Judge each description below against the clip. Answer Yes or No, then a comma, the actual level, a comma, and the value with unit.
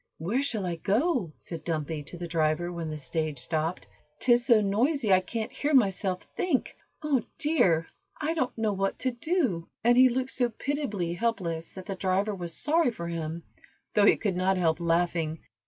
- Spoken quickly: No, average, 185 wpm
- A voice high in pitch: Yes, high, 195 Hz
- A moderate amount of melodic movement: No, wide, 6.6 semitones